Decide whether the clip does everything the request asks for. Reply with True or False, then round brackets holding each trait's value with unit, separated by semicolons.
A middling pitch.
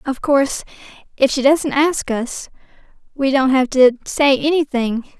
False (270 Hz)